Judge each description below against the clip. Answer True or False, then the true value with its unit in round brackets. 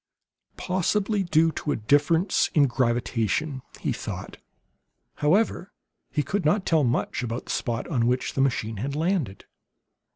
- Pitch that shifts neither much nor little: False (5.9 semitones)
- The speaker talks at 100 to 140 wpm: True (135 wpm)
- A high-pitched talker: False (145 Hz)